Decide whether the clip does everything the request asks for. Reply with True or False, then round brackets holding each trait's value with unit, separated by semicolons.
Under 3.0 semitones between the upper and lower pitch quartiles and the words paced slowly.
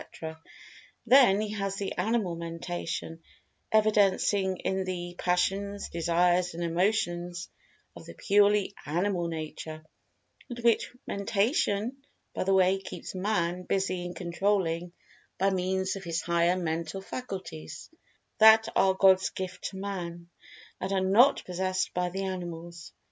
True (2.5 semitones; 125 wpm)